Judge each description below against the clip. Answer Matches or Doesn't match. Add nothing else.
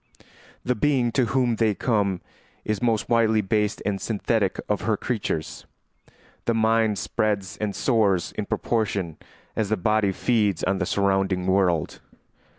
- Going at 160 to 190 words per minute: Doesn't match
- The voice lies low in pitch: Matches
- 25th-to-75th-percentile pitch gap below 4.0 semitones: Matches